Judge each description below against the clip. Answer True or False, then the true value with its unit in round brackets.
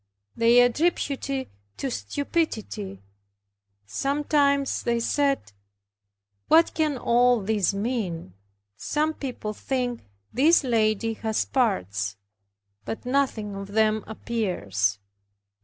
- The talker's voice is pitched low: False (235 Hz)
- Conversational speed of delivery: False (95 wpm)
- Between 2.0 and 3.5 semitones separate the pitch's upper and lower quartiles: False (5.2 semitones)